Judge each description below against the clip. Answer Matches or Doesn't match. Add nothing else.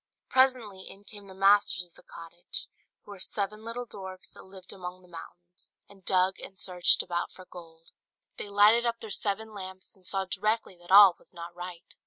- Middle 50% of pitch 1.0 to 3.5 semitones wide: Matches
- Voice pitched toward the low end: Doesn't match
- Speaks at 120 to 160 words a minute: Doesn't match